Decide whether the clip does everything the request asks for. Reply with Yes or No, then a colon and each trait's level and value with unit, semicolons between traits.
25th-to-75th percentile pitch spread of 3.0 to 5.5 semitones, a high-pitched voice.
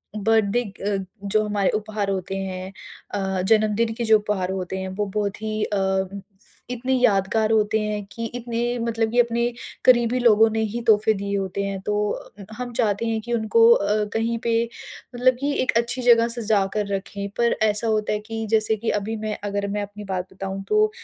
No: narrow, 2.6 semitones; high, 215 Hz